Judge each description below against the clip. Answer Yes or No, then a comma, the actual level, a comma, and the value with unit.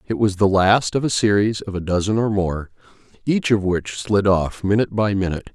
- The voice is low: Yes, low, 100 Hz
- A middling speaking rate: No, fast, 215 wpm